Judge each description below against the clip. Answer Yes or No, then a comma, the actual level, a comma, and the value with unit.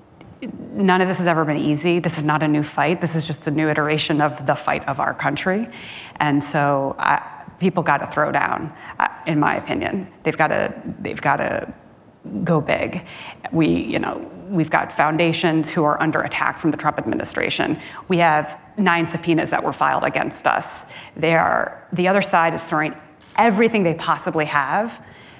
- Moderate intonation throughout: Yes, average, 3.1 semitones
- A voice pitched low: No, medium, 165 Hz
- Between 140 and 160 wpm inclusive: No, average, 180 wpm